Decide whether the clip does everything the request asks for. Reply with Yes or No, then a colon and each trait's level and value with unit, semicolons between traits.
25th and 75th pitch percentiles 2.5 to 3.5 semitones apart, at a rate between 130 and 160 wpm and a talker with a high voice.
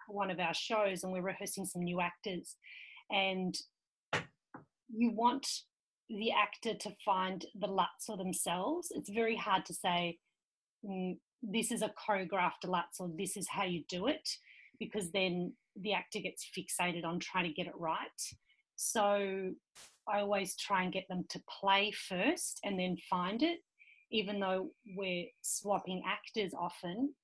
Yes: average, 2.9 semitones; average, 155 wpm; high, 195 Hz